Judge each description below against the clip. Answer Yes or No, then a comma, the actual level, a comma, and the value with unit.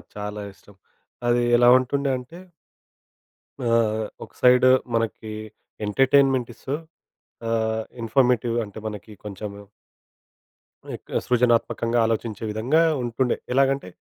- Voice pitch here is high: No, low, 115 Hz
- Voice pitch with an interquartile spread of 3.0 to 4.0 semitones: No, narrow, 2.6 semitones